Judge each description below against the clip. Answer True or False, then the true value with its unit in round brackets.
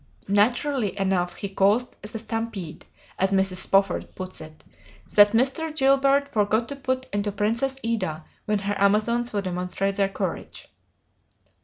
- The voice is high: True (205 Hz)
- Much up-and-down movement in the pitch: False (3.7 semitones)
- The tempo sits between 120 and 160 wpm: True (140 wpm)